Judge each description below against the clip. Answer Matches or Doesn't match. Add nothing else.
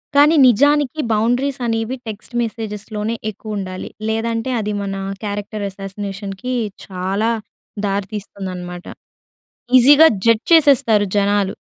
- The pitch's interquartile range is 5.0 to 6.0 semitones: Doesn't match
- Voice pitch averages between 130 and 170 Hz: Doesn't match